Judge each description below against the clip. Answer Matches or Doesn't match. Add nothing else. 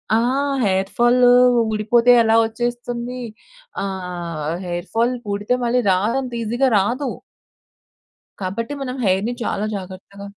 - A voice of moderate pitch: Doesn't match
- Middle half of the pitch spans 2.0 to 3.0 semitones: Doesn't match